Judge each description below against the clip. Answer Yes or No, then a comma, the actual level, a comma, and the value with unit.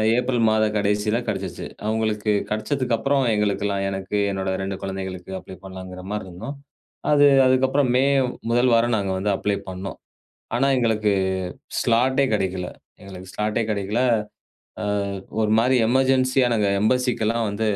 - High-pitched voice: No, low, 105 Hz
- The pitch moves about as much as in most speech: Yes, average, 4.1 semitones